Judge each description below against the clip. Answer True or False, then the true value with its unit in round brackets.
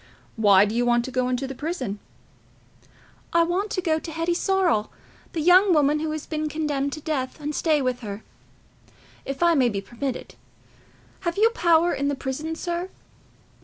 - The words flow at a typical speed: True (180 wpm)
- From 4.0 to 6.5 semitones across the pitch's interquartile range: True (5.0 semitones)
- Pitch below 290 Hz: False (300 Hz)